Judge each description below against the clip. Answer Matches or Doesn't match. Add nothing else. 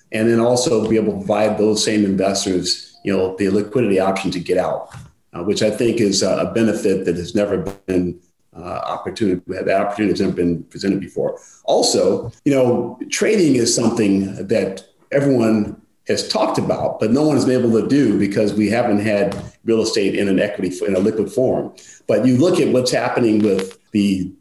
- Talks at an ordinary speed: Matches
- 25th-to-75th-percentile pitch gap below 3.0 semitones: Matches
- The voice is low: Matches